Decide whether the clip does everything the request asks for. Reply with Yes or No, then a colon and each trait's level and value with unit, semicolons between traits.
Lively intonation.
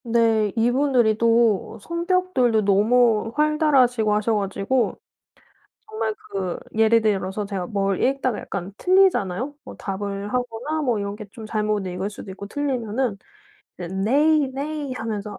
No: average, 4.5 semitones